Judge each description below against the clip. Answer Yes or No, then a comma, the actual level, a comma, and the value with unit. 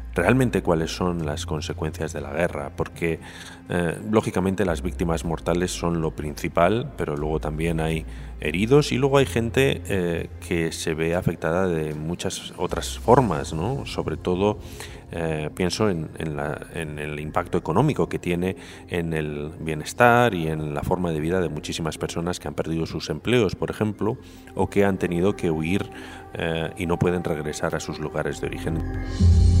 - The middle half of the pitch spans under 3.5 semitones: Yes, average, 2.8 semitones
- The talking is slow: No, average, 170 wpm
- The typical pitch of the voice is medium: No, very low, 85 Hz